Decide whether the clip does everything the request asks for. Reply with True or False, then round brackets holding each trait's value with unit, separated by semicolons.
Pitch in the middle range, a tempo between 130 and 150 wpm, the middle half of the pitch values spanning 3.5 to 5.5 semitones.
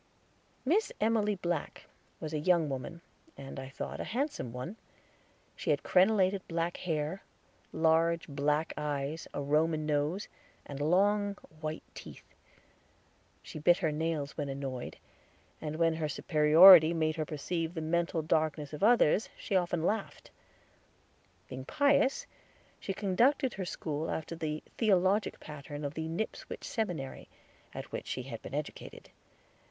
True (160 Hz; 140 wpm; 4.0 semitones)